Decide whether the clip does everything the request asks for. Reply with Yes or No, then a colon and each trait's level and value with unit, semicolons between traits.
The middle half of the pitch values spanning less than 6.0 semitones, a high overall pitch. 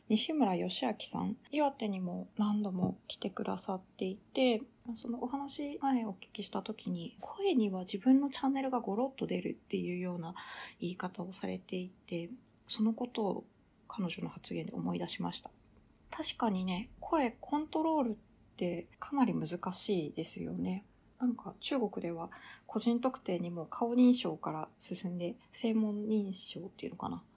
Yes: average, 5.1 semitones; high, 215 Hz